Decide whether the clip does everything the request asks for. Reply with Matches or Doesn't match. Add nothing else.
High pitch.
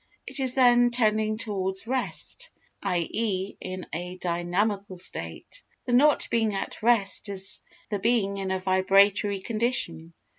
Matches